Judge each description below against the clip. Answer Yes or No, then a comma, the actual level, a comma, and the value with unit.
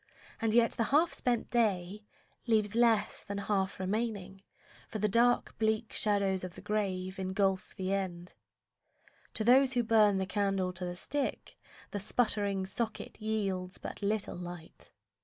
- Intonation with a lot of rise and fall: No, average, 2.8 semitones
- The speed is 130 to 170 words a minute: Yes, average, 150 wpm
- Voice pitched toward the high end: Yes, high, 205 Hz